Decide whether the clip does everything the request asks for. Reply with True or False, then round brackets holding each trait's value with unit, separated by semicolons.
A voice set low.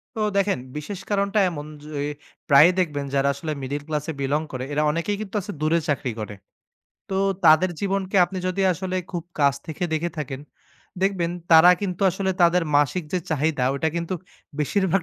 False (165 Hz)